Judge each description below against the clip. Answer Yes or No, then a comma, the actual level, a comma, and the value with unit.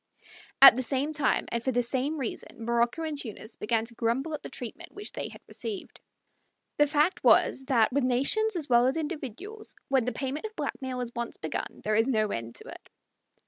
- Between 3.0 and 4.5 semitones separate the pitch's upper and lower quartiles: Yes, average, 4.2 semitones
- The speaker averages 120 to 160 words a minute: No, average, 200 wpm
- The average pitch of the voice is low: No, very high, 260 Hz